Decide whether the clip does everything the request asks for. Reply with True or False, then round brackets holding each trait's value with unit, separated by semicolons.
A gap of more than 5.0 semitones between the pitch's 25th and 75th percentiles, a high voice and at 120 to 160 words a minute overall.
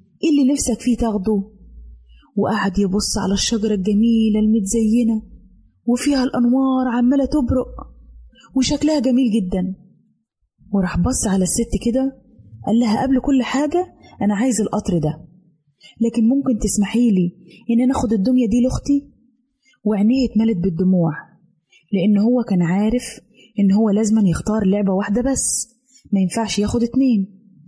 False (4.1 semitones; 220 Hz; 130 wpm)